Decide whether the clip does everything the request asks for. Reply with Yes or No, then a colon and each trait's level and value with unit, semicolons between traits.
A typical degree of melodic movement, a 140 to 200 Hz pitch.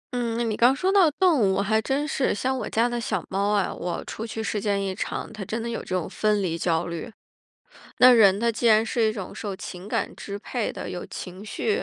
No: average, 3.4 semitones; high, 220 Hz